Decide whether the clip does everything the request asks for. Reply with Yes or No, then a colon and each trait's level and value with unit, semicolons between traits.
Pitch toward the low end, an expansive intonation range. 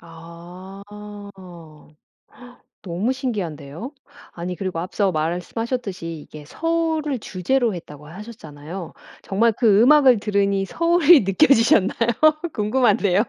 No: high, 200 Hz; wide, 6.0 semitones